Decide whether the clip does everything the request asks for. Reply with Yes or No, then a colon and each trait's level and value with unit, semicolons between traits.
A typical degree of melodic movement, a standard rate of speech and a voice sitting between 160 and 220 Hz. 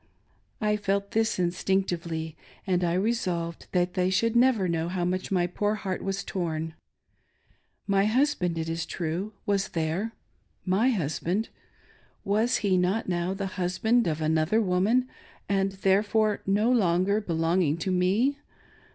Yes: average, 3.4 semitones; average, 145 wpm; high, 190 Hz